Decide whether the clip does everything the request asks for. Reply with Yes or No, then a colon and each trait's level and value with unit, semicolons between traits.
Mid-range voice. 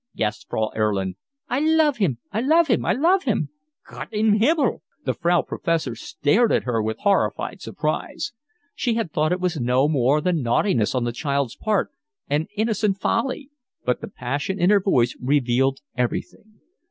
Yes: medium, 165 Hz